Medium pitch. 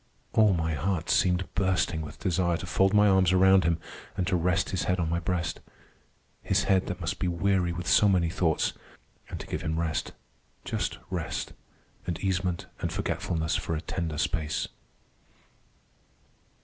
No: very low, 90 Hz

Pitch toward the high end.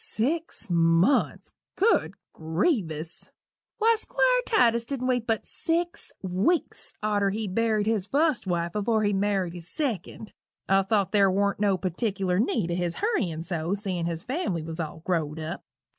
Yes: high, 200 Hz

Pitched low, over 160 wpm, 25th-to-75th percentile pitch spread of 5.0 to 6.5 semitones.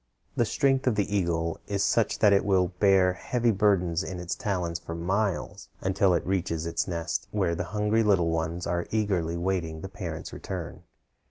No: very low, 95 Hz; average, 180 wpm; average, 3.3 semitones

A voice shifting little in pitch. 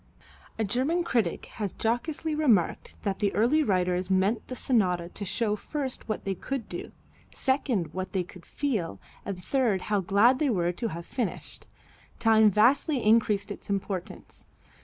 No: average, 5.2 semitones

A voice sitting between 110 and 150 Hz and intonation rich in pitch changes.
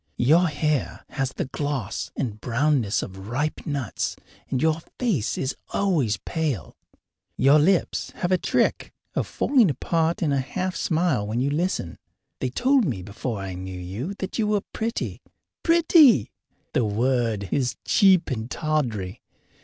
Yes: medium, 140 Hz; wide, 7.5 semitones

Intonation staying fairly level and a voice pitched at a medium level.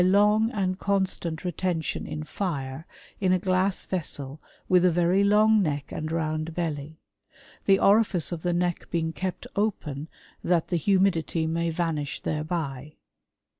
No: average, 3.3 semitones; medium, 175 Hz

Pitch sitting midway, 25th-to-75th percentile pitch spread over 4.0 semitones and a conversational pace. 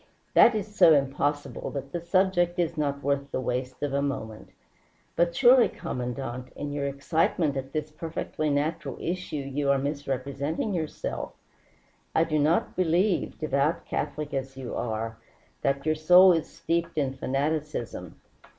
No: medium, 145 Hz; average, 3.3 semitones; average, 150 wpm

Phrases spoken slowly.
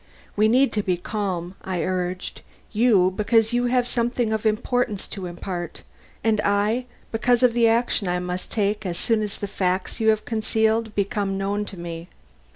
No: average, 175 wpm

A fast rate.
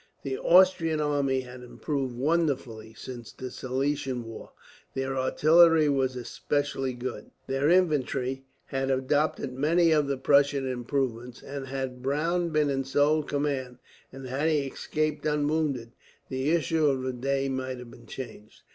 No: average, 145 wpm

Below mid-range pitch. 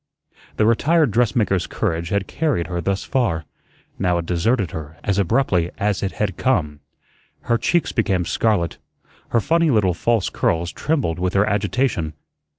Yes: low, 100 Hz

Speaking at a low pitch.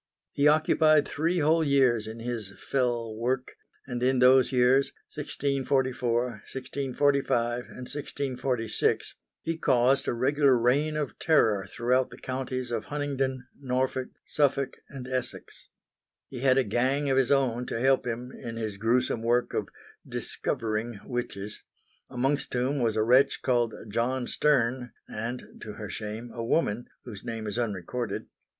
Yes: low, 125 Hz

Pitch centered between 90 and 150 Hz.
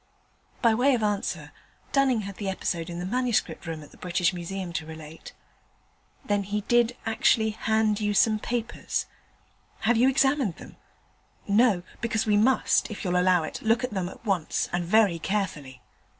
No: high, 205 Hz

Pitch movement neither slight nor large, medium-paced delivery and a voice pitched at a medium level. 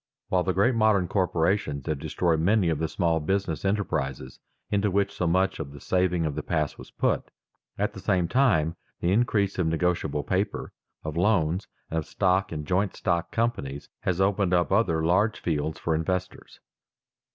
No: average, 3.6 semitones; average, 175 wpm; very low, 90 Hz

